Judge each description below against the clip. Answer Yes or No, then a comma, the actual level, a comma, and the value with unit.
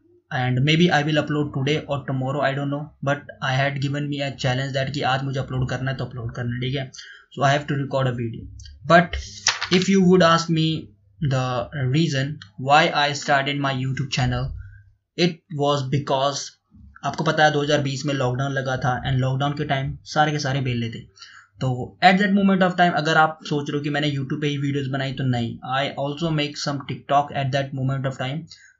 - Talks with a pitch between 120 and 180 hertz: Yes, medium, 140 Hz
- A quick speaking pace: Yes, fast, 215 wpm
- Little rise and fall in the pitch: Yes, narrow, 2.2 semitones